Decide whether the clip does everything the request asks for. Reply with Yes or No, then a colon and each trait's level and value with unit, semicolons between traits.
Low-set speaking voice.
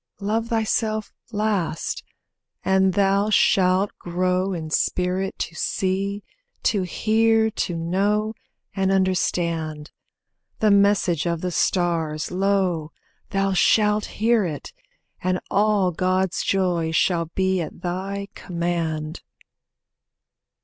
No: high, 190 Hz